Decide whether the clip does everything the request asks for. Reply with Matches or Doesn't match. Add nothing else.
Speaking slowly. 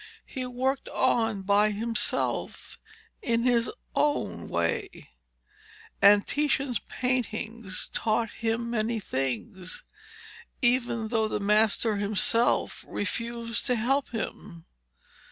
Matches